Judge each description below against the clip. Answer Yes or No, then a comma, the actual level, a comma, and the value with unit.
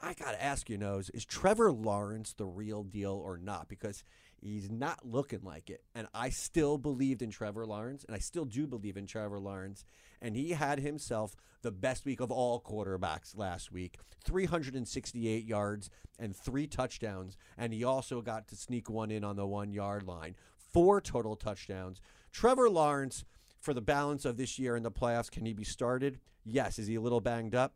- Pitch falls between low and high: No, low, 110 Hz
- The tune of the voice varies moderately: Yes, average, 4.3 semitones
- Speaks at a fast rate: No, average, 195 wpm